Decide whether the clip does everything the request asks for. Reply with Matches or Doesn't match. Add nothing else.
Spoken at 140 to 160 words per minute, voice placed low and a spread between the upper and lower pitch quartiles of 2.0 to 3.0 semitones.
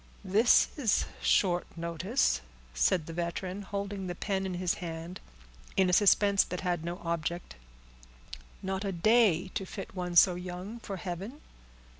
Doesn't match